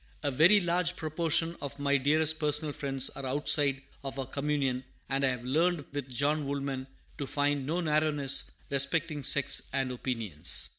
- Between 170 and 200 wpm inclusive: No, average, 160 wpm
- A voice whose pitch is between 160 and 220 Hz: No, medium, 140 Hz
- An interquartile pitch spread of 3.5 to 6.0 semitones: No, narrow, 2.4 semitones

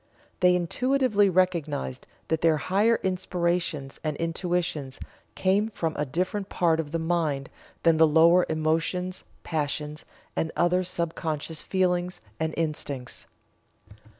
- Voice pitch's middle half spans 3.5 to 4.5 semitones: No, average, 2.7 semitones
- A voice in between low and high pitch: Yes, medium, 165 Hz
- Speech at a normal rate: No, slow, 125 wpm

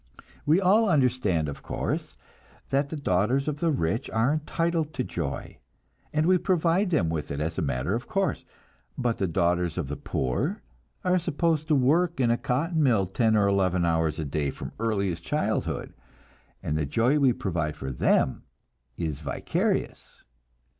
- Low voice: Yes, low, 115 Hz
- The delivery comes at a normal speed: Yes, average, 165 wpm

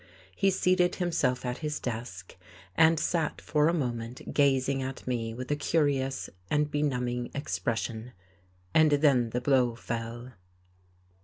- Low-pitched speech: Yes, low, 130 Hz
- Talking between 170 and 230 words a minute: No, slow, 135 wpm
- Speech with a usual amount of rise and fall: Yes, average, 3.7 semitones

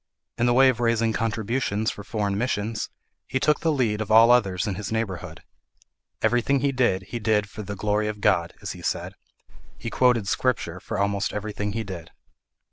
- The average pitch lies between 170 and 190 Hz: No, low, 110 Hz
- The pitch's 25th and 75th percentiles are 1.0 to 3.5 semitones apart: Yes, average, 3.0 semitones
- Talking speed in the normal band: Yes, average, 190 wpm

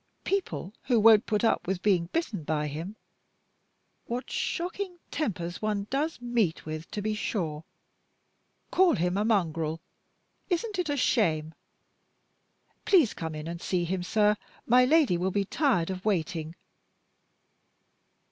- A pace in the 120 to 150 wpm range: Yes, average, 140 wpm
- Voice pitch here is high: Yes, high, 205 Hz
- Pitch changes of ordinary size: No, wide, 6.8 semitones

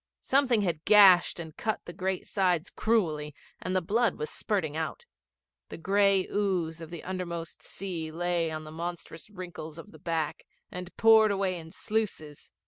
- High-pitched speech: No, medium, 180 Hz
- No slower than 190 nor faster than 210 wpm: No, average, 165 wpm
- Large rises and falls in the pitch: No, average, 3.6 semitones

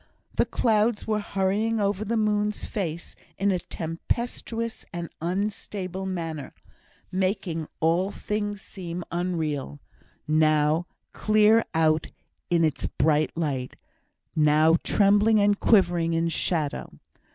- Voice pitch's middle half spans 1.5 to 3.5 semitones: No, average, 4.4 semitones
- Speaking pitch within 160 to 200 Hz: Yes, medium, 185 Hz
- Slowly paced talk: Yes, slow, 110 wpm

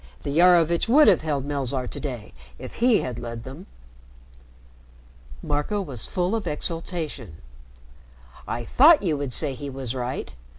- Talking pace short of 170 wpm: Yes, average, 145 wpm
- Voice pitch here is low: No, medium, 145 Hz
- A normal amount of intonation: No, wide, 5.7 semitones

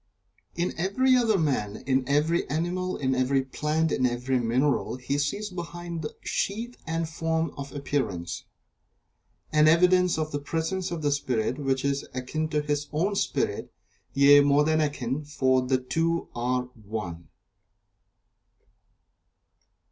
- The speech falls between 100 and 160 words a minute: Yes, average, 140 wpm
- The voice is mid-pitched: Yes, medium, 145 Hz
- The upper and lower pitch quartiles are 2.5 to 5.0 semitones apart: Yes, average, 4.1 semitones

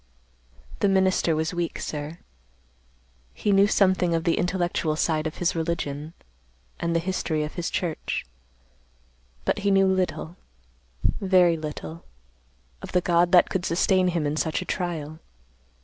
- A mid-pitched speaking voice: Yes, medium, 170 Hz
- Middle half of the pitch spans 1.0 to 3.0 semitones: Yes, average, 2.7 semitones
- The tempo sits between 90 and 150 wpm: Yes, average, 145 wpm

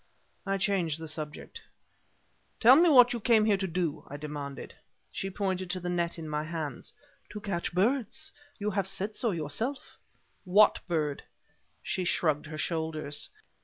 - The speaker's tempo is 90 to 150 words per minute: No, average, 160 wpm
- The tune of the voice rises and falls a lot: No, average, 5.0 semitones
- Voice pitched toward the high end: No, medium, 180 Hz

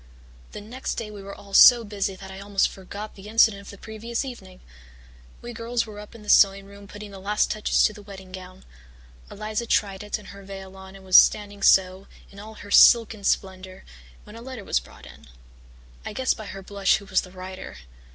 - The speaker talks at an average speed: No, fast, 215 wpm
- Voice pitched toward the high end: Yes, high, 200 Hz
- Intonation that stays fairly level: Yes, narrow, 1.8 semitones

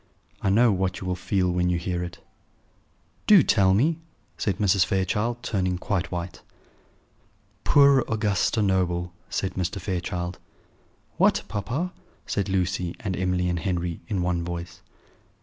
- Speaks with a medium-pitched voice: No, very low, 95 Hz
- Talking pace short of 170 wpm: Yes, average, 140 wpm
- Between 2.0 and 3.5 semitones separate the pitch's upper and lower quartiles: Yes, narrow, 2.5 semitones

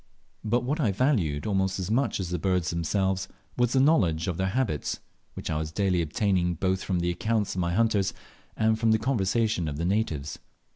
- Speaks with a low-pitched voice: Yes, very low, 95 Hz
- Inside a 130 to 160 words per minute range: No, average, 200 wpm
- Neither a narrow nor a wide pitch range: Yes, average, 4.3 semitones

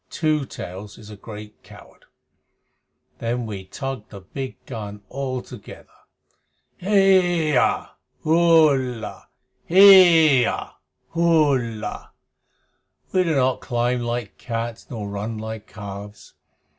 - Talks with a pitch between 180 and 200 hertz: No, low, 125 Hz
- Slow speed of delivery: Yes, slow, 100 wpm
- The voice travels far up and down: Yes, wide, 6.5 semitones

